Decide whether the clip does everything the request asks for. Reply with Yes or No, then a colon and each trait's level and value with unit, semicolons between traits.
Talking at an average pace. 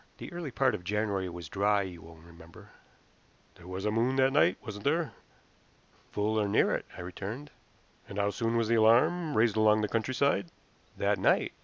Yes: average, 185 wpm